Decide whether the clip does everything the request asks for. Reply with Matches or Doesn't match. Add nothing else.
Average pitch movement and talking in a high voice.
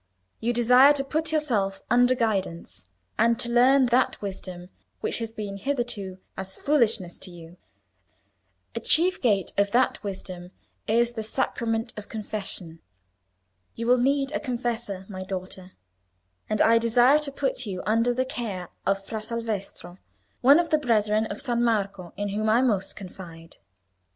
Matches